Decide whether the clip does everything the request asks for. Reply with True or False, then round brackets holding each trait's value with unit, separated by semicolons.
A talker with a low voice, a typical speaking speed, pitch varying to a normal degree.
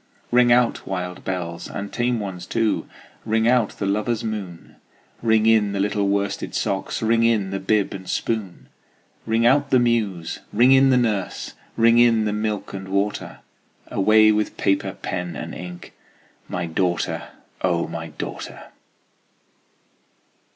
True (105 Hz; 145 wpm; 3.3 semitones)